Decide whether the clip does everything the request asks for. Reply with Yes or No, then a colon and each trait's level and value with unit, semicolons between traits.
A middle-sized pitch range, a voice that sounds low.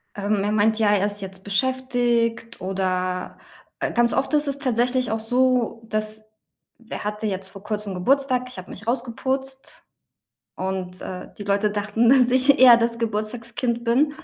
No: average, 3.6 semitones; high, 225 Hz